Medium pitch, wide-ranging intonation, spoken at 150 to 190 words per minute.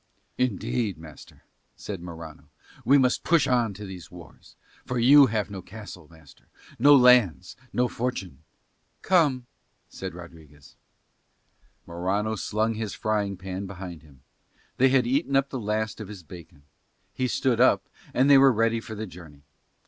No: low, 105 Hz; wide, 6.0 semitones; average, 155 wpm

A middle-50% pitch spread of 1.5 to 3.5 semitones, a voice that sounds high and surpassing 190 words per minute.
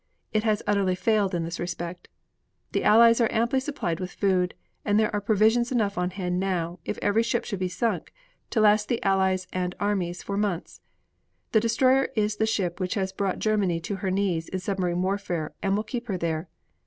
Yes: average, 3.1 semitones; high, 200 Hz; average, 200 wpm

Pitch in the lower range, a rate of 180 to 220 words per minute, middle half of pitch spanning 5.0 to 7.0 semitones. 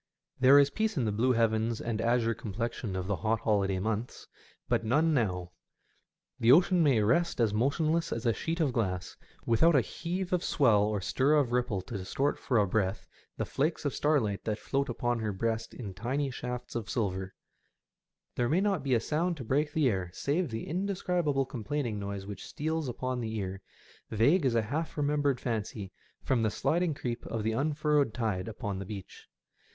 Yes: low, 120 Hz; average, 190 wpm; wide, 5.5 semitones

